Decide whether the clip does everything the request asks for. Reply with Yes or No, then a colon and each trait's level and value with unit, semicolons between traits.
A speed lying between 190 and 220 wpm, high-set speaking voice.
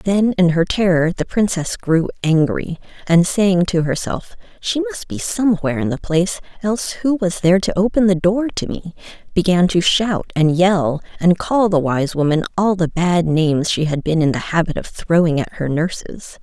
No: average, 195 wpm; medium, 175 Hz